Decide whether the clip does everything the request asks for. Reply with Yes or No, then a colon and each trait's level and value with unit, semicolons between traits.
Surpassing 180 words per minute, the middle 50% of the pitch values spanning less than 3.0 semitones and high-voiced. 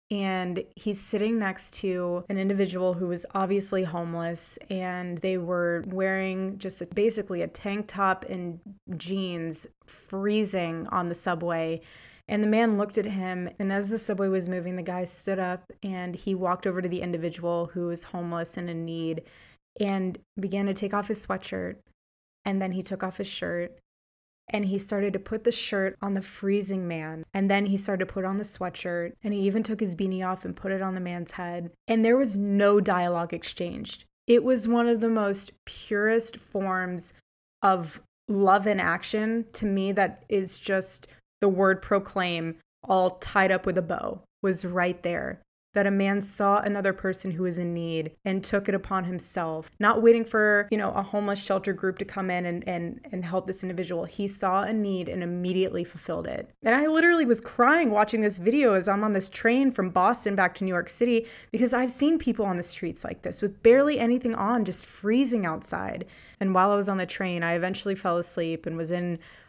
Yes: average, 200 wpm; narrow, 2.4 semitones; high, 195 Hz